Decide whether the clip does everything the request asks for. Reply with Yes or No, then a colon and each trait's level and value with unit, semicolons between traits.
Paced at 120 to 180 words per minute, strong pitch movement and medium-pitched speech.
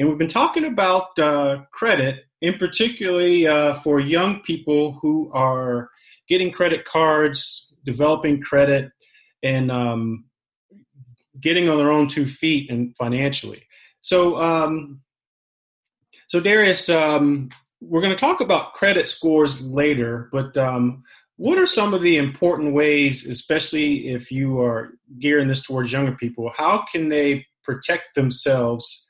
No: slow, 135 wpm; average, 3.7 semitones; medium, 145 Hz